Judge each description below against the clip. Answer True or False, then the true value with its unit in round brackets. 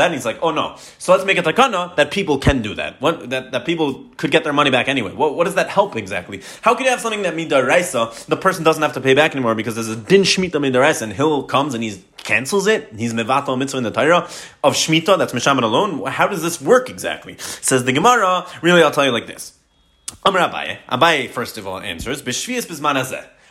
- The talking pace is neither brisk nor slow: False (235 wpm)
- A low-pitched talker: False (145 Hz)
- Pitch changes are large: True (5.7 semitones)